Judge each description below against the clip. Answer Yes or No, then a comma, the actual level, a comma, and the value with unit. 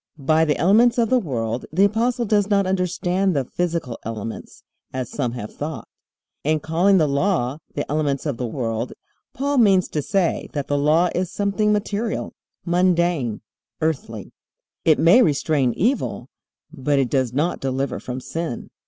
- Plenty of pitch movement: Yes, wide, 6.2 semitones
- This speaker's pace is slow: No, average, 160 wpm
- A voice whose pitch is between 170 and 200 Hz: No, medium, 160 Hz